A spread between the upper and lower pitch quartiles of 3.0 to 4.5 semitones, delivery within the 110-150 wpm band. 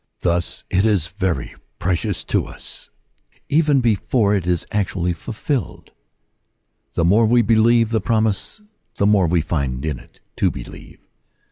No: average, 4.9 semitones; average, 140 wpm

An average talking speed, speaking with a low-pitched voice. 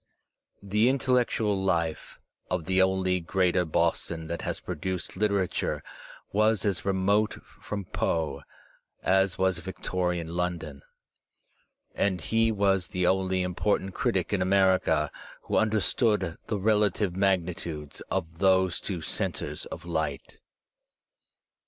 No: slow, 115 wpm; very low, 95 Hz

